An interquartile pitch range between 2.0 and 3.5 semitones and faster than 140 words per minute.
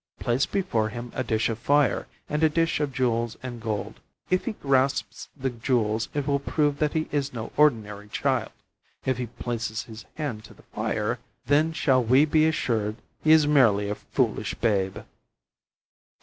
No: average, 4.7 semitones; average, 175 wpm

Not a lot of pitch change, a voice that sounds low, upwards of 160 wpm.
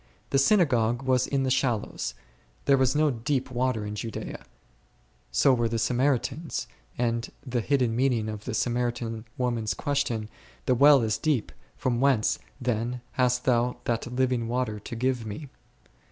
No: narrow, 2.3 semitones; low, 125 Hz; average, 155 wpm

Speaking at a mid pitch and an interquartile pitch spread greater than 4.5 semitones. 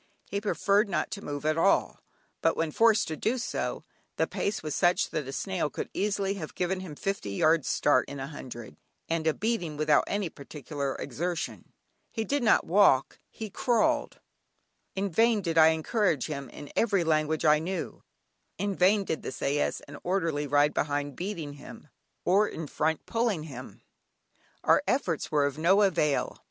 Yes: medium, 165 Hz; average, 5.2 semitones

